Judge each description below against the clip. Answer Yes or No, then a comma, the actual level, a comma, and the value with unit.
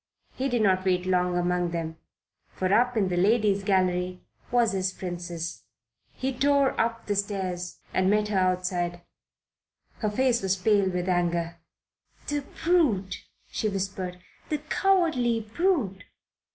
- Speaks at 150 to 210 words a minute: No, average, 140 wpm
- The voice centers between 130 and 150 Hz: No, high, 195 Hz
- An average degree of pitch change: Yes, average, 4.4 semitones